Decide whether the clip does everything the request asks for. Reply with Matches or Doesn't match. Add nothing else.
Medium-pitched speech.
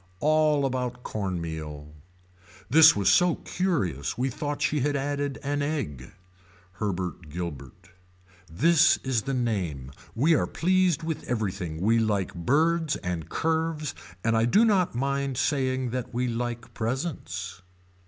Doesn't match